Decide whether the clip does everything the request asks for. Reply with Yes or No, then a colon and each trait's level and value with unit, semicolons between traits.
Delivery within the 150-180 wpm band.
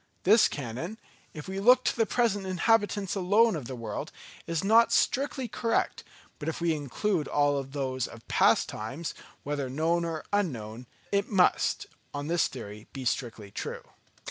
Yes: average, 160 wpm